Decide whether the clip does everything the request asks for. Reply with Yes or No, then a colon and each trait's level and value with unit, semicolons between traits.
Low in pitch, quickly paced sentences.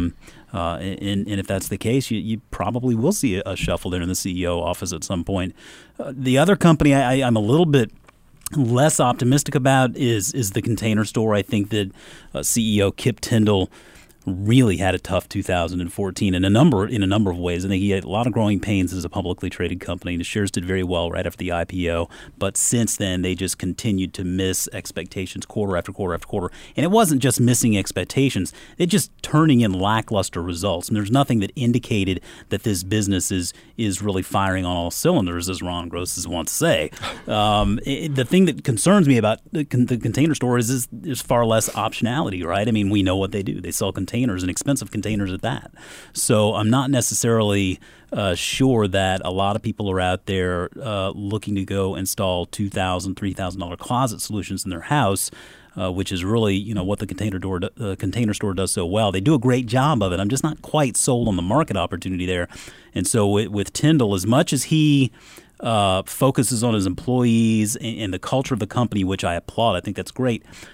Yes: low, 100 Hz; fast, 210 wpm